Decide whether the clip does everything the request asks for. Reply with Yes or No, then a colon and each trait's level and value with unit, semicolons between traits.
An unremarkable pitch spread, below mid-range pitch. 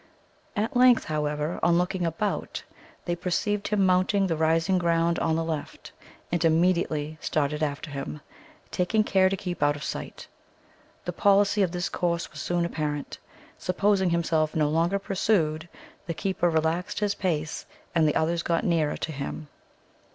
No: average, 3.2 semitones; medium, 170 Hz